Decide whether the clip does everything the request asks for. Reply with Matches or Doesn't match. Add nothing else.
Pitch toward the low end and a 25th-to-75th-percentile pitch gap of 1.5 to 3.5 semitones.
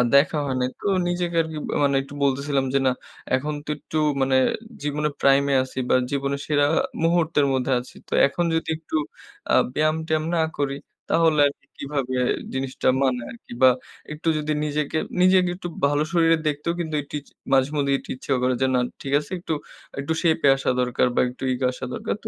Doesn't match